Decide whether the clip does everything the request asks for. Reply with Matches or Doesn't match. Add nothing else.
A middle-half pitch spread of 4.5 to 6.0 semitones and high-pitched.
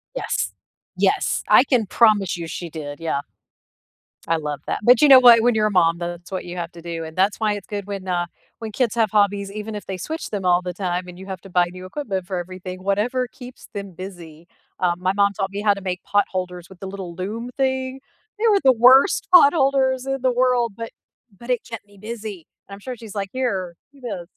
Matches